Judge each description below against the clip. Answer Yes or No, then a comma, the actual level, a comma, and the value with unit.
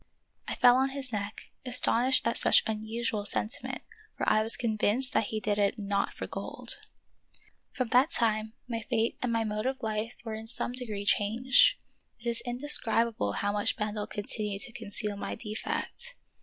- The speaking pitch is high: Yes, high, 225 Hz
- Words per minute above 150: Yes, average, 170 wpm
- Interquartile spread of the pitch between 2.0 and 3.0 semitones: Yes, narrow, 2.6 semitones